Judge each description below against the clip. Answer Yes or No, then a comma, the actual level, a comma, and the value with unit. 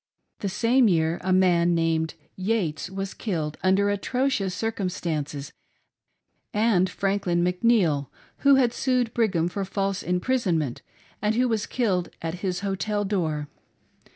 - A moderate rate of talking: No, slow, 130 wpm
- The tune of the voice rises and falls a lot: No, average, 4.2 semitones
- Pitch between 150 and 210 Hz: Yes, high, 190 Hz